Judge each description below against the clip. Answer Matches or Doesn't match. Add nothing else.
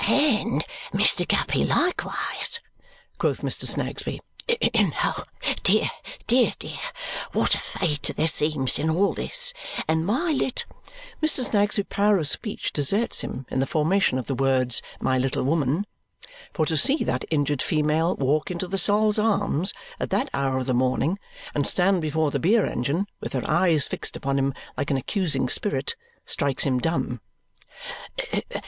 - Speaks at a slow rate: Doesn't match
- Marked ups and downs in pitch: Matches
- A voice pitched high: Doesn't match